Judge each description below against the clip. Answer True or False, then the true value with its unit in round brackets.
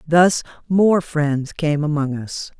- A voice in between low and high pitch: True (155 Hz)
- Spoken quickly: False (140 wpm)